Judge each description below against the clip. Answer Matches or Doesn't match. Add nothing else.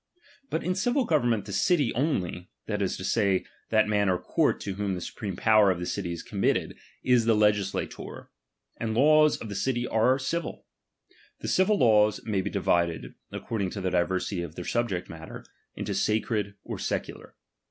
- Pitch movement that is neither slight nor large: Matches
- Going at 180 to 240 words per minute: Matches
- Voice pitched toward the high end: Doesn't match